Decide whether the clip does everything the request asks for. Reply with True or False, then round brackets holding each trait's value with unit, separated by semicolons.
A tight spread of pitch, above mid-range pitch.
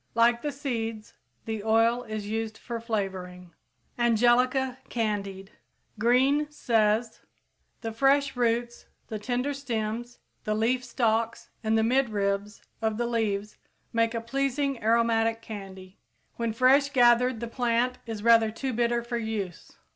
True (2.1 semitones; 230 Hz)